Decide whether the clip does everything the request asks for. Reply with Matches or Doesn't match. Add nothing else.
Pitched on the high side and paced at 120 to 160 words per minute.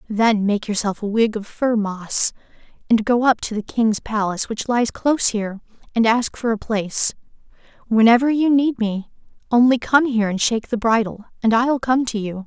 Doesn't match